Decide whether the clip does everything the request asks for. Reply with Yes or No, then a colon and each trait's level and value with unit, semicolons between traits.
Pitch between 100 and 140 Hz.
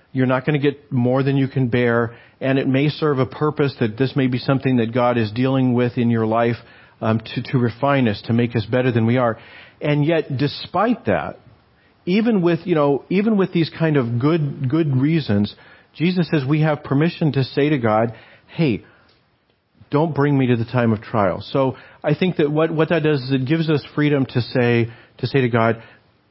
Yes: low, 135 Hz